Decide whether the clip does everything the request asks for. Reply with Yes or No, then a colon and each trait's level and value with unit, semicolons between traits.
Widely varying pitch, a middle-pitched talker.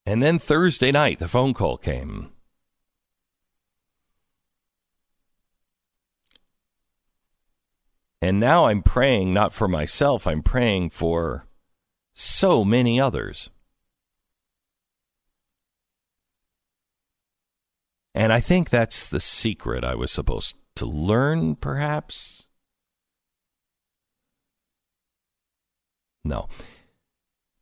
No: wide, 7.8 semitones; low, 110 Hz